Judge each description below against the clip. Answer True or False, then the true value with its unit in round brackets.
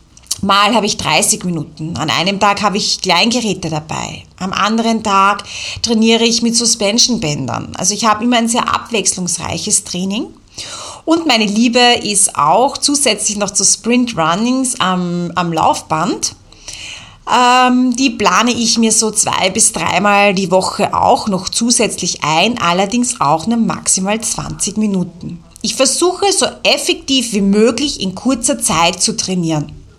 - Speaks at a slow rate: False (145 wpm)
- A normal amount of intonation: True (4.1 semitones)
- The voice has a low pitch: False (210 Hz)